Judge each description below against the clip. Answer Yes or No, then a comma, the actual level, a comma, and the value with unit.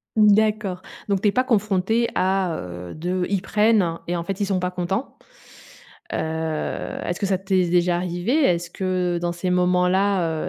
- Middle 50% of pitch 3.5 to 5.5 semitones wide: No, narrow, 2.4 semitones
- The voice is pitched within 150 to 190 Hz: Yes, medium, 185 Hz